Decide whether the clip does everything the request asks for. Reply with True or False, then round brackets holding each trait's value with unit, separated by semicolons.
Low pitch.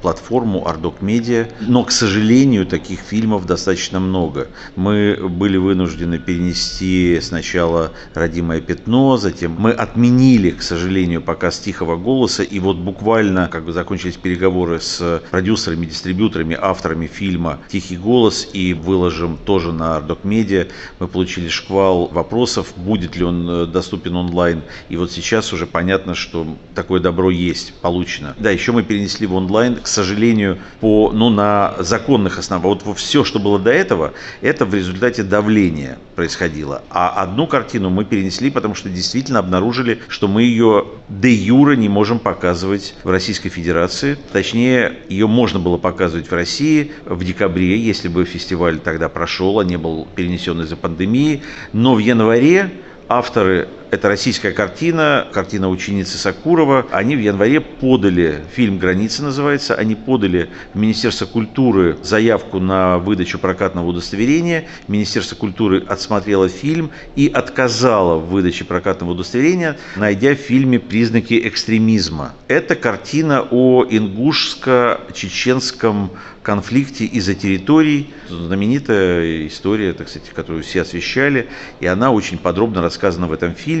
True (95 Hz)